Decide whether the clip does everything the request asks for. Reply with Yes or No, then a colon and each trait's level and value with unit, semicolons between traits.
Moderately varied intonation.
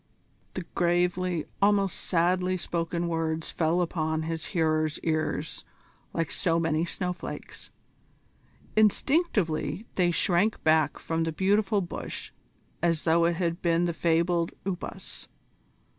No: narrow, 2.0 semitones